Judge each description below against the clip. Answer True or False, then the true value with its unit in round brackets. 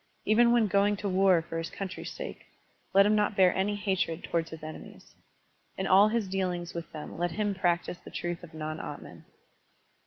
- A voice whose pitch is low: False (190 Hz)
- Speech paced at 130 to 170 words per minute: False (190 wpm)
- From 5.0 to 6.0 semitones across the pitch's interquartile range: False (3.2 semitones)